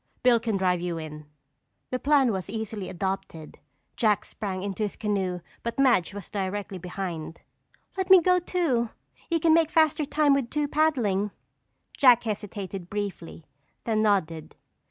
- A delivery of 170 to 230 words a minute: No, average, 150 wpm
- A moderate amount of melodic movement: No, wide, 6.4 semitones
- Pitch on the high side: Yes, high, 210 Hz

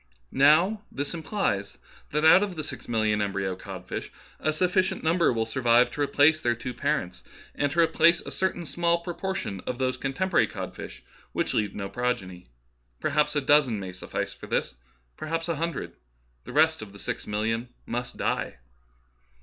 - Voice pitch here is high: No, medium, 140 Hz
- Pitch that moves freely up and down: Yes, wide, 7.1 semitones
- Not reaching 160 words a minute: No, average, 170 wpm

